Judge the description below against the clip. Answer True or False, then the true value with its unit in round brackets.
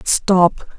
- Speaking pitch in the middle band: True (180 Hz)